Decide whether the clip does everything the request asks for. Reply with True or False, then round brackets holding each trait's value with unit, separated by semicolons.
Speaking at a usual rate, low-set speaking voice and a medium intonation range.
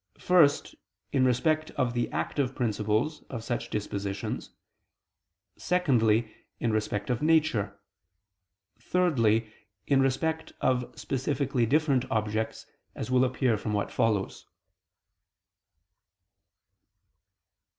False (95 wpm; 125 Hz; 4.6 semitones)